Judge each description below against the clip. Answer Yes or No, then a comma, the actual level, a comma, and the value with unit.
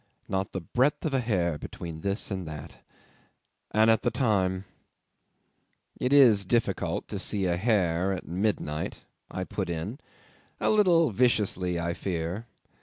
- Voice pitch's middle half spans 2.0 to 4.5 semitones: No, average, 5.3 semitones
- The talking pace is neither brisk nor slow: Yes, average, 150 wpm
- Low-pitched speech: Yes, very low, 95 Hz